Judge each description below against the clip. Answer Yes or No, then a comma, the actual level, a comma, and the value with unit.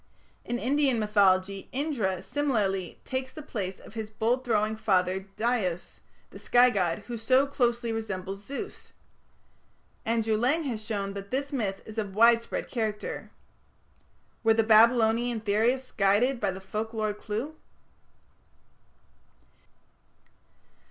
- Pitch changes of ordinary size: Yes, average, 3.4 semitones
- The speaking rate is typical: No, slow, 125 wpm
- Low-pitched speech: No, high, 220 Hz